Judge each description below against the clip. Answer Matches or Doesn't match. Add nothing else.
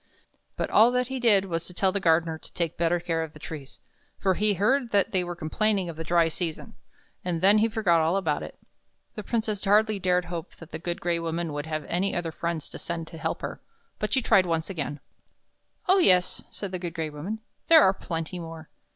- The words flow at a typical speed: Doesn't match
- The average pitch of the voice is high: Doesn't match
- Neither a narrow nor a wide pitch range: Matches